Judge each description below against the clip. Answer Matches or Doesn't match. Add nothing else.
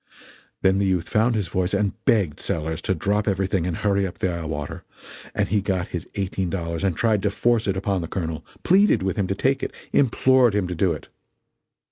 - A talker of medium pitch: Doesn't match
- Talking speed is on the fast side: Matches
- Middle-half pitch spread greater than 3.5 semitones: Doesn't match